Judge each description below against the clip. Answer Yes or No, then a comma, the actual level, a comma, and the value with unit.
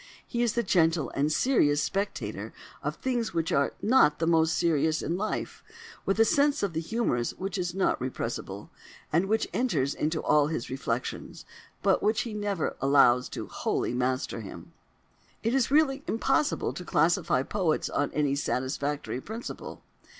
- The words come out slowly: No, average, 155 wpm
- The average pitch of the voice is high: No, medium, 165 Hz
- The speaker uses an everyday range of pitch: No, wide, 7.6 semitones